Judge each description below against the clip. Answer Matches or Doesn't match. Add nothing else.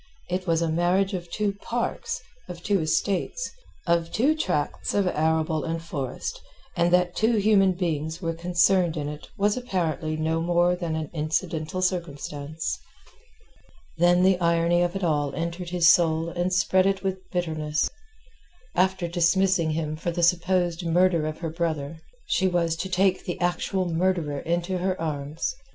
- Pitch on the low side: Doesn't match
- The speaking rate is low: Doesn't match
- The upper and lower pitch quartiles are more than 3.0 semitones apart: Doesn't match